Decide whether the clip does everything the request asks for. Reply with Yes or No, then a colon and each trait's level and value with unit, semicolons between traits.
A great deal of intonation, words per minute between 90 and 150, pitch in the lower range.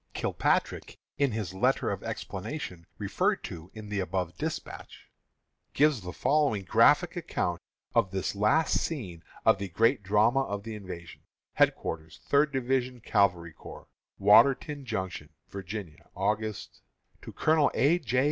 Yes: wide, 6.2 semitones; slow, 135 wpm; low, 105 Hz